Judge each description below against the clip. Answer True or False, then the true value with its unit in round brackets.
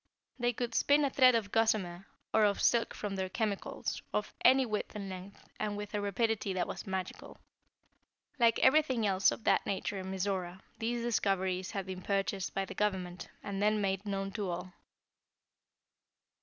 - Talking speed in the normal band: True (170 wpm)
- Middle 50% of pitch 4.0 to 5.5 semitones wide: False (2.9 semitones)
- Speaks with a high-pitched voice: True (200 Hz)